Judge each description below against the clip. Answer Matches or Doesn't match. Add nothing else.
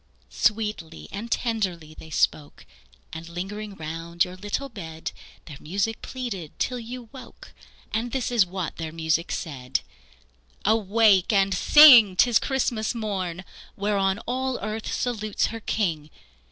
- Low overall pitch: Doesn't match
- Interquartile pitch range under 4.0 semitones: Doesn't match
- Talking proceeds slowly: Matches